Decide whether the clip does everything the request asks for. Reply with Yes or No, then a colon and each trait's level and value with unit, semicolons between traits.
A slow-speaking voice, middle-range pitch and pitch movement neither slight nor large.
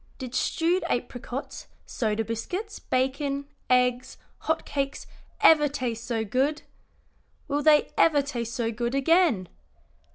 No: slow, 120 wpm; very high, 265 Hz; average, 3.8 semitones